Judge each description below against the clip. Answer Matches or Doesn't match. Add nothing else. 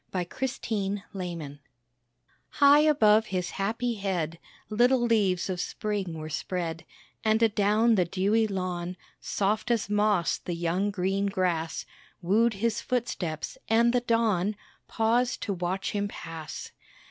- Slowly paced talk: Matches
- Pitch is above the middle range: Matches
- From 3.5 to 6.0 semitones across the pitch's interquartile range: Matches